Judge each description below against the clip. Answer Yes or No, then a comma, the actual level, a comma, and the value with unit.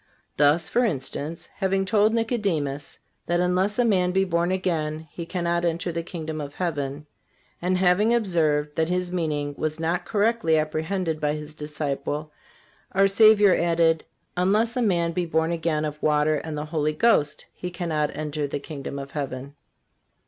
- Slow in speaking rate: No, average, 165 wpm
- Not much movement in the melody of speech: No, average, 3.4 semitones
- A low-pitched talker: No, medium, 165 Hz